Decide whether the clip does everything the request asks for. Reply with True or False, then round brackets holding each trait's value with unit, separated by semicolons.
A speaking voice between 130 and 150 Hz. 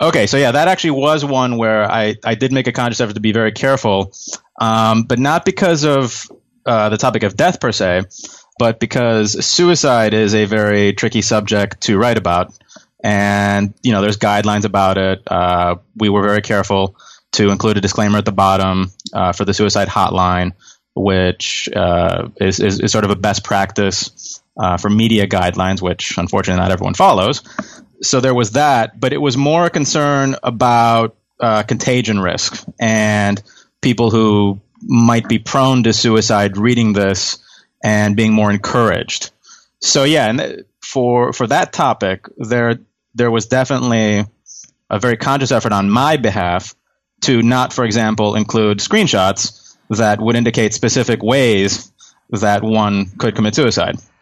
False (110 Hz)